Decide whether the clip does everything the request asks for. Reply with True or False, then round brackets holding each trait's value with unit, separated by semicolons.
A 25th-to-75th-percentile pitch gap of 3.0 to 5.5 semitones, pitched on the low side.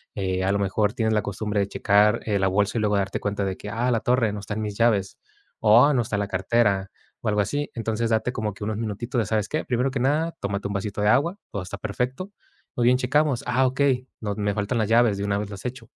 True (3.4 semitones; 110 Hz)